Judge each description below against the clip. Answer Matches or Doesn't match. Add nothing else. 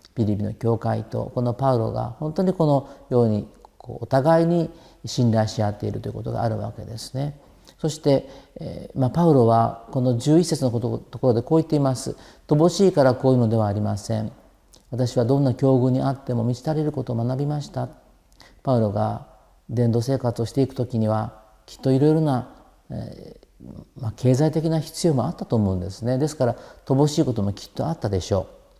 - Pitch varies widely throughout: Doesn't match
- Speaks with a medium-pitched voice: Doesn't match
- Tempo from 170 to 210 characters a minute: Doesn't match